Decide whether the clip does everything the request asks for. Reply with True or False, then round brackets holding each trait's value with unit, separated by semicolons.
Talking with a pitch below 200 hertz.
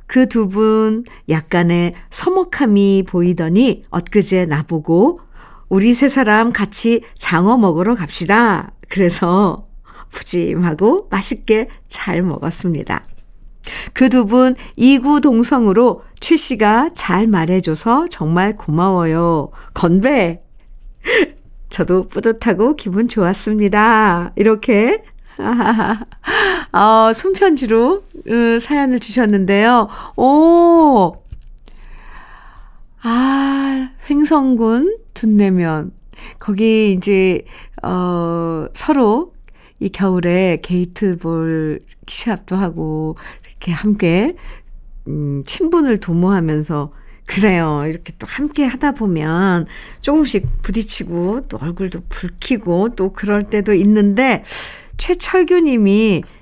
False (210 Hz)